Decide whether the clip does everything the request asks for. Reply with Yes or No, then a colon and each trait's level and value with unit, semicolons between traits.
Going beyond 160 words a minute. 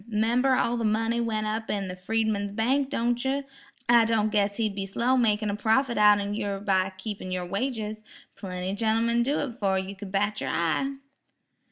Yes: average, 190 wpm